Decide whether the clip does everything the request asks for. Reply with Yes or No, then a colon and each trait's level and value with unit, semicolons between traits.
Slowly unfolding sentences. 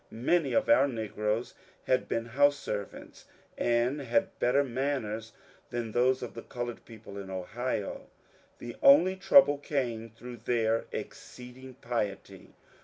Yes: slow, 130 wpm